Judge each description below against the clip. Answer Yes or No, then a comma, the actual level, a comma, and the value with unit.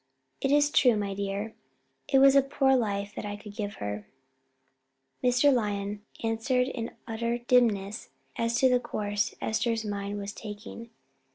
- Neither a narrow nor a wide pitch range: Yes, average, 3.4 semitones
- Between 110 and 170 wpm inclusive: Yes, average, 155 wpm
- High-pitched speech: Yes, high, 225 Hz